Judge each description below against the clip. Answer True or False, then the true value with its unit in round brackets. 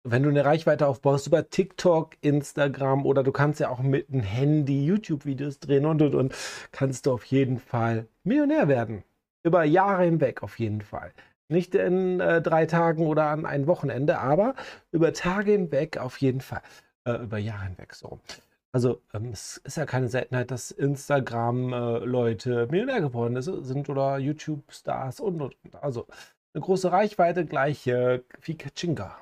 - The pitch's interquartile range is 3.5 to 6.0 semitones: True (4.3 semitones)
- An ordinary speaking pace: True (165 wpm)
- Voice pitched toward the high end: False (140 Hz)